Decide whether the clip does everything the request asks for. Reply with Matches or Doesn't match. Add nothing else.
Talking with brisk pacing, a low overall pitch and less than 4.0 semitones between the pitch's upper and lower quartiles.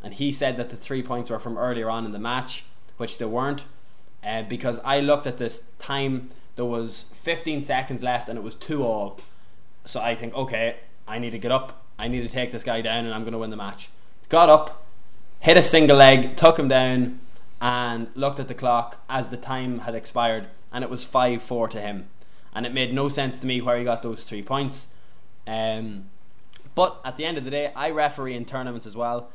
Matches